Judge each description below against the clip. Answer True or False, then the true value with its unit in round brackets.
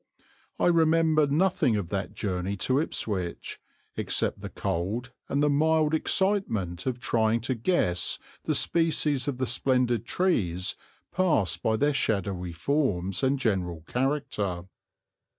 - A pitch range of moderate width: False (7.6 semitones)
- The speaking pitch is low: True (125 Hz)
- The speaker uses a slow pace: True (130 wpm)